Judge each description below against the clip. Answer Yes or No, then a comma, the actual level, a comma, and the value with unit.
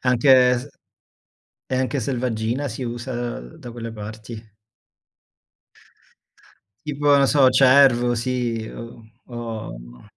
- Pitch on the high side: No, low, 120 Hz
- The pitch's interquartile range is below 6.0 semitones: Yes, narrow, 2.4 semitones